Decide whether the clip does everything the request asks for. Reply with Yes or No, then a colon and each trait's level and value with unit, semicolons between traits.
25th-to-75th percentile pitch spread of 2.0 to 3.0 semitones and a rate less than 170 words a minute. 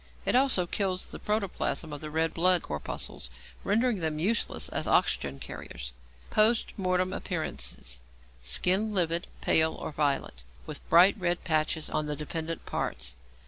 No: average, 3.9 semitones; average, 145 wpm